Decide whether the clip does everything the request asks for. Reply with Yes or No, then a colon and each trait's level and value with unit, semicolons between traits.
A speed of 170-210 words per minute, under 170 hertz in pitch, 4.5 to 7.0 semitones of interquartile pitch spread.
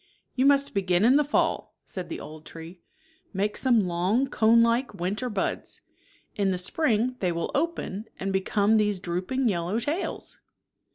No: average, 175 wpm; high, 210 Hz; wide, 5.5 semitones